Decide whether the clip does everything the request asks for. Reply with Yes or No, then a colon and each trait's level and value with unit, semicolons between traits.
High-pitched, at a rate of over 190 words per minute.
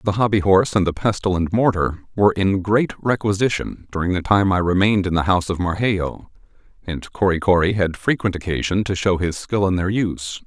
No: very low, 95 Hz; average, 200 wpm